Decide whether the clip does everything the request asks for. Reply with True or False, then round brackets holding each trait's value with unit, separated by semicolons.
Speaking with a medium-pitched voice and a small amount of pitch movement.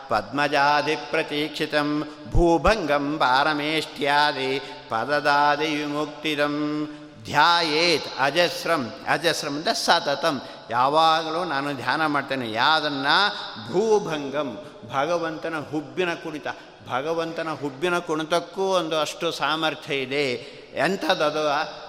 True (150 Hz; 1.7 semitones)